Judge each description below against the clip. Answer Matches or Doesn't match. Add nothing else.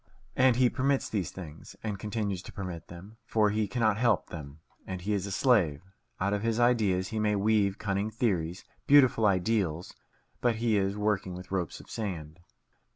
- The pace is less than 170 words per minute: Doesn't match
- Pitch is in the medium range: Doesn't match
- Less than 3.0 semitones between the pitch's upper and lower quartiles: Doesn't match